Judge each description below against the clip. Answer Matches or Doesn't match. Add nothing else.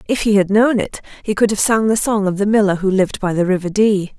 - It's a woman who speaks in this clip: Matches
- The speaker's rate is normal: Doesn't match